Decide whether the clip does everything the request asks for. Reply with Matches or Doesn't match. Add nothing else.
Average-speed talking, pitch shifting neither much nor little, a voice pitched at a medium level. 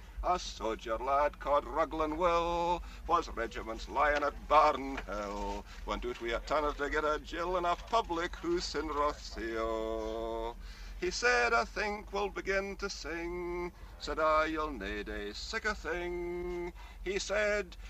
Doesn't match